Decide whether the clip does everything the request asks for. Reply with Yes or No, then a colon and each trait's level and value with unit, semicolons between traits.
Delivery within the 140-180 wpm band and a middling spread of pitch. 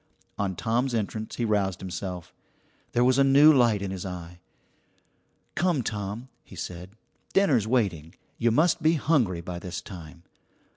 No: average, 150 wpm; wide, 6.0 semitones